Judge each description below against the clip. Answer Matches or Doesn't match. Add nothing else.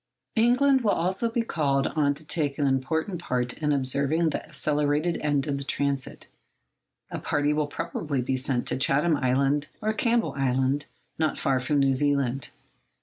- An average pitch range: Matches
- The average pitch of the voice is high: Doesn't match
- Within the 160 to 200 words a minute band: Matches